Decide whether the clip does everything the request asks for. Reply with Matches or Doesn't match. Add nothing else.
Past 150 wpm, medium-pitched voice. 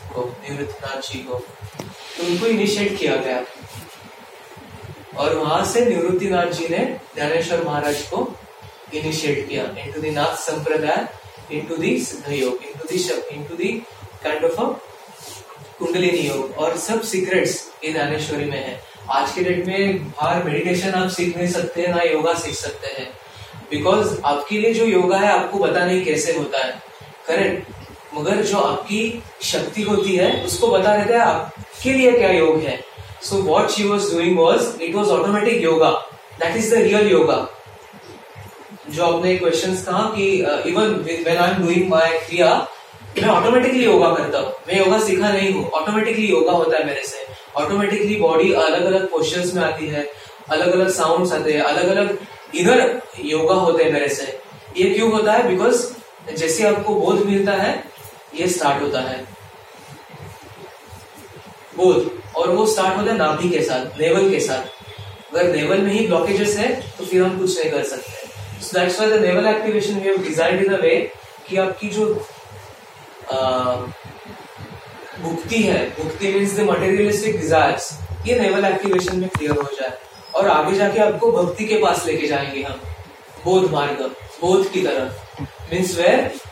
Doesn't match